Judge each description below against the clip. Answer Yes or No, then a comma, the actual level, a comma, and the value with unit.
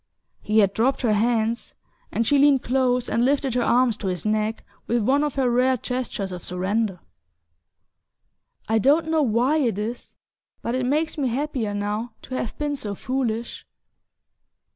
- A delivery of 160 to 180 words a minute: Yes, average, 165 wpm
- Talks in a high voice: Yes, high, 240 Hz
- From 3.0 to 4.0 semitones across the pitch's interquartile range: Yes, average, 3.6 semitones